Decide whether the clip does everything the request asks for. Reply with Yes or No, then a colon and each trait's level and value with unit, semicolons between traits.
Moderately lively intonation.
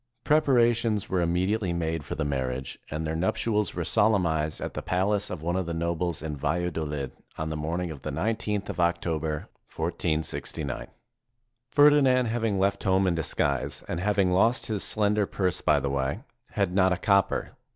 Yes: average, 4.7 semitones